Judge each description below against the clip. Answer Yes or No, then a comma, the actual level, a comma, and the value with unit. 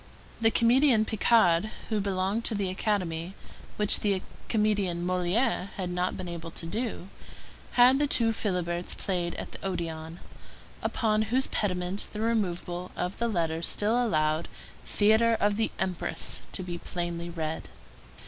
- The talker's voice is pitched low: No, high, 190 Hz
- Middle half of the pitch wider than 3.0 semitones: Yes, average, 4.1 semitones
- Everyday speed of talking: Yes, average, 145 wpm